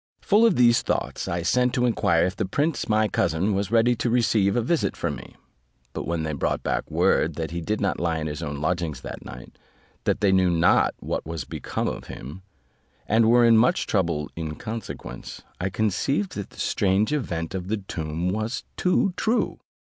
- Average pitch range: No, wide, 5.8 semitones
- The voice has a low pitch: Yes, very low, 95 Hz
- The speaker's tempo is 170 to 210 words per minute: Yes, average, 200 wpm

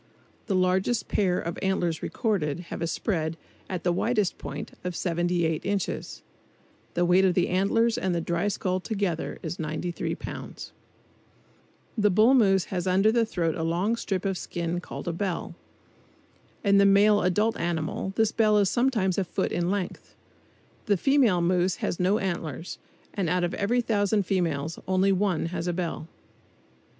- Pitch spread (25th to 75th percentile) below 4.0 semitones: Yes, average, 2.9 semitones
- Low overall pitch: No, medium, 185 Hz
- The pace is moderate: Yes, average, 165 wpm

